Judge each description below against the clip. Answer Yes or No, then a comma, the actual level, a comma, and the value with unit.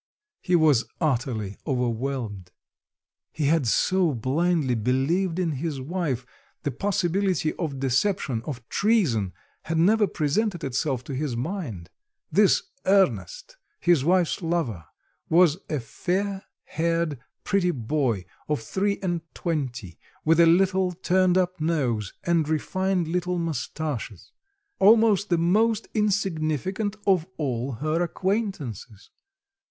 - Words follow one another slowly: Yes, slow, 115 wpm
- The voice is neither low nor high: Yes, medium, 165 Hz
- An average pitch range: No, wide, 6.0 semitones